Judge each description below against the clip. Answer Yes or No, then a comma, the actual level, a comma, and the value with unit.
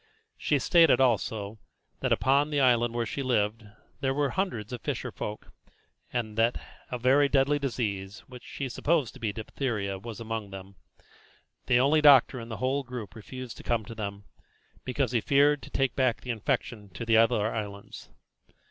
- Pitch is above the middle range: No, low, 120 Hz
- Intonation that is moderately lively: Yes, average, 3.6 semitones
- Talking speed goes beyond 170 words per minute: Yes, average, 180 wpm